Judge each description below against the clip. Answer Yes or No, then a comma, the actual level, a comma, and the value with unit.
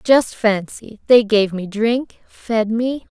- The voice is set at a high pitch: Yes, high, 225 Hz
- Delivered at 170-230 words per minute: No, average, 155 wpm